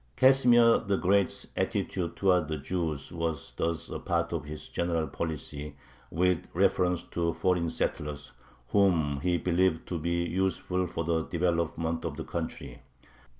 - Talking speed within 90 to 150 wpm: Yes, average, 145 wpm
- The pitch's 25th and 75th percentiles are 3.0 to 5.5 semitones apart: No, narrow, 2.5 semitones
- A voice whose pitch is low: Yes, very low, 85 Hz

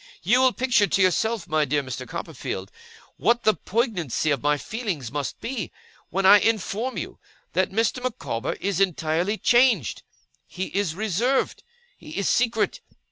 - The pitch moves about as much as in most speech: No, wide, 6.6 semitones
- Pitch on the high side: Yes, high, 200 Hz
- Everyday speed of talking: Yes, average, 150 wpm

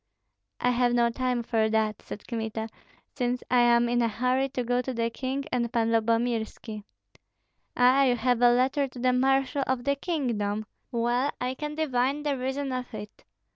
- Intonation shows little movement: Yes, narrow, 2.1 semitones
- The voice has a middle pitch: No, high, 245 Hz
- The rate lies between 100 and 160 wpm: No, average, 180 wpm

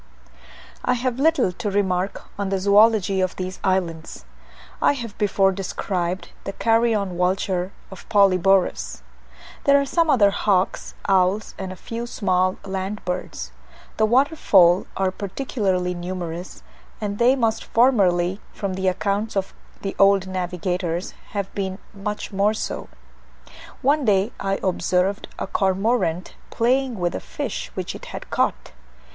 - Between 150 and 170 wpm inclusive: No, average, 140 wpm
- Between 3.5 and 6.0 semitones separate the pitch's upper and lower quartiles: No, average, 2.8 semitones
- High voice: Yes, high, 195 Hz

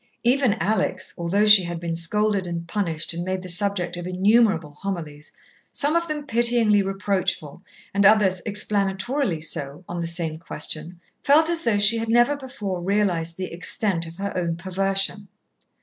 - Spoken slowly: No, average, 165 wpm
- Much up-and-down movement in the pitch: No, average, 3.9 semitones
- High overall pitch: Yes, high, 195 Hz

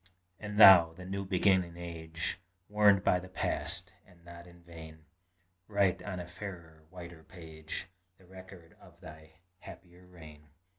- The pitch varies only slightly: Yes, narrow, 2.2 semitones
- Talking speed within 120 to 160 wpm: Yes, average, 145 wpm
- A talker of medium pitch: No, very low, 85 Hz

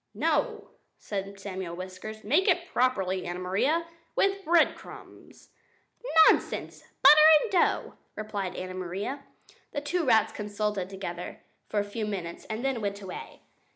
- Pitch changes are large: Yes, wide, 6.6 semitones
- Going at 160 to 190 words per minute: No, slow, 135 wpm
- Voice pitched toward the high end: Yes, high, 205 Hz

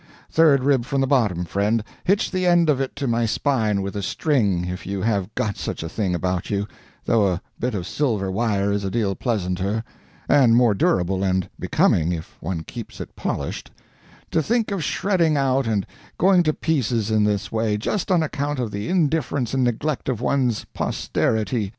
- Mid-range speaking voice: No, low, 115 Hz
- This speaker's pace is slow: No, average, 190 wpm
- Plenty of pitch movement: Yes, wide, 6.0 semitones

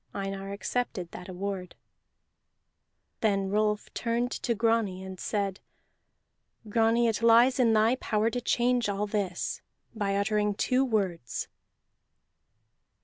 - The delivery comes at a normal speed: No, slow, 115 wpm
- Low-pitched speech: No, high, 210 Hz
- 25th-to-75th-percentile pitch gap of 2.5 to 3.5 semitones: Yes, average, 2.8 semitones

